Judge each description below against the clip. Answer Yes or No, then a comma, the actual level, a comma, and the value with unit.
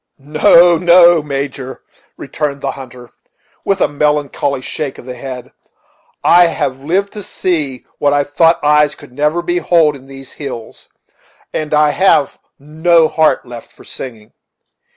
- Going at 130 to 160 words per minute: Yes, average, 145 wpm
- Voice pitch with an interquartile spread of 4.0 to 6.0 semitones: No, average, 3.5 semitones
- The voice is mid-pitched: Yes, medium, 150 Hz